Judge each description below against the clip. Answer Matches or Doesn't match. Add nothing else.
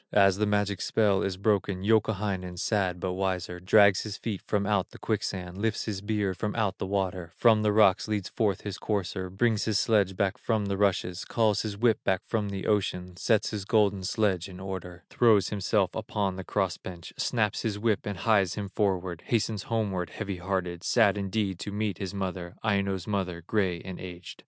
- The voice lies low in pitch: Matches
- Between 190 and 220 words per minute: Matches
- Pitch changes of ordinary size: Doesn't match